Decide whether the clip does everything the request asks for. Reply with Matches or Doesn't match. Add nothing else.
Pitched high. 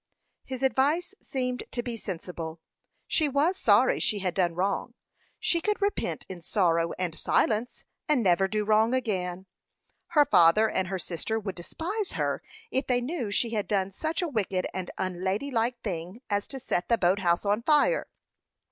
Matches